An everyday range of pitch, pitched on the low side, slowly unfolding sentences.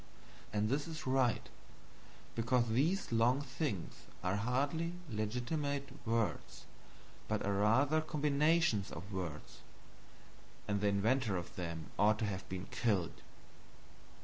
No: wide, 5.9 semitones; low, 115 Hz; slow, 120 wpm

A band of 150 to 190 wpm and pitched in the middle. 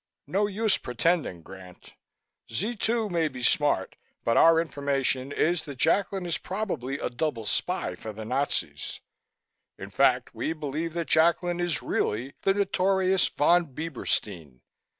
No: average, 140 wpm; medium, 155 Hz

